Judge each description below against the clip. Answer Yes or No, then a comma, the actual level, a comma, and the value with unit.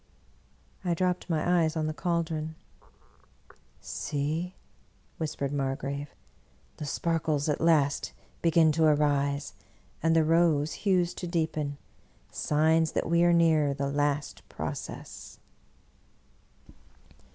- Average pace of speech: No, slow, 115 wpm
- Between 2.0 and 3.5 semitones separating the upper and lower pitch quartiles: Yes, narrow, 2.6 semitones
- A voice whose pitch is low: No, medium, 155 Hz